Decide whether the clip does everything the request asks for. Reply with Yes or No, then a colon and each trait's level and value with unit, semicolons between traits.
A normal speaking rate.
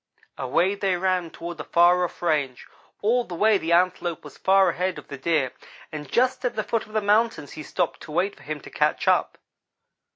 No: fast, 215 wpm